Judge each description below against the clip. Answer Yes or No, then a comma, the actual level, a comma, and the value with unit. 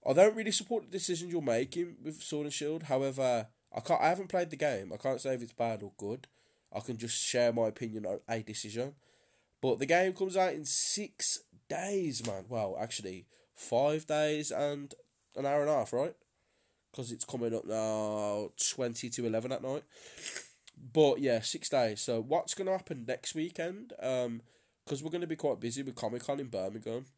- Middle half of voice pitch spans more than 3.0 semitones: Yes, wide, 5.6 semitones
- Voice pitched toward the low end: Yes, low, 130 Hz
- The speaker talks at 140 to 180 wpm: No, average, 200 wpm